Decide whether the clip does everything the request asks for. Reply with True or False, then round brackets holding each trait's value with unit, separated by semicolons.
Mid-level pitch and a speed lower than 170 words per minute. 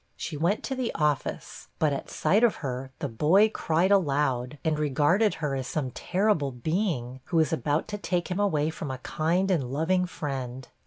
False (155 Hz; 190 wpm)